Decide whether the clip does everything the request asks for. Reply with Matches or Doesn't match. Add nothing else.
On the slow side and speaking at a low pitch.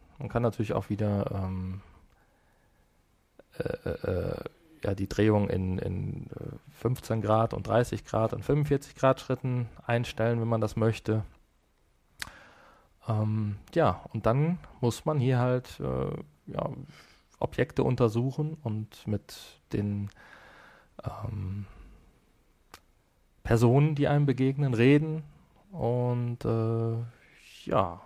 Matches